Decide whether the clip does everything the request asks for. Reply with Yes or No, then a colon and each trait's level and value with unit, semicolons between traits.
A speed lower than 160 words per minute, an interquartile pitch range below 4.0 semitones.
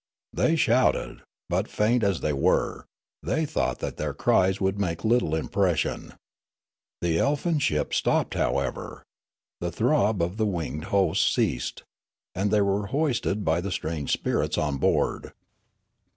No: average, 140 wpm; average, 5.2 semitones